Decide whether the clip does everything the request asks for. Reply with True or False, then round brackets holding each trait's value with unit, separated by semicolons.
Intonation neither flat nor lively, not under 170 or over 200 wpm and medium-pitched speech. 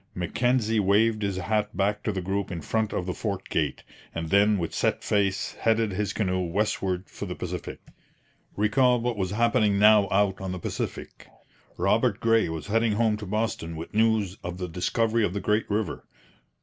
False (3.0 semitones; 185 wpm; 105 Hz)